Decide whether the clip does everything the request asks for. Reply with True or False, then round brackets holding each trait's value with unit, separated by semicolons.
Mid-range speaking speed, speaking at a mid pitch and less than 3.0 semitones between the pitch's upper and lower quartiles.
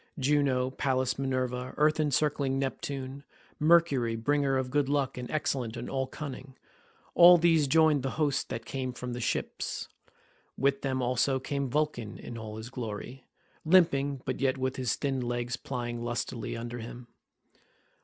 False (150 wpm; 130 Hz; 2.5 semitones)